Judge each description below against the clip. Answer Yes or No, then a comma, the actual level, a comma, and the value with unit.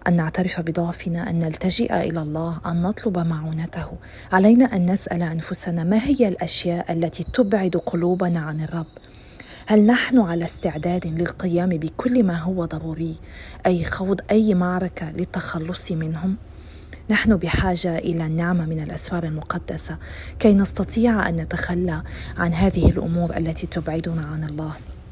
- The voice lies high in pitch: No, medium, 175 Hz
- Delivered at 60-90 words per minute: No, average, 130 wpm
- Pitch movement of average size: No, narrow, 2.1 semitones